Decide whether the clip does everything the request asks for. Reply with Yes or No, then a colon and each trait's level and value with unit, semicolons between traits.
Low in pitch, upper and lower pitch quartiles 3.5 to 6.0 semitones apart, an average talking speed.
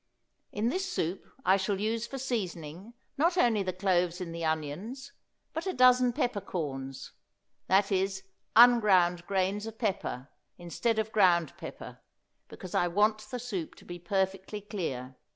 No: high, 195 Hz; average, 4.6 semitones; average, 150 wpm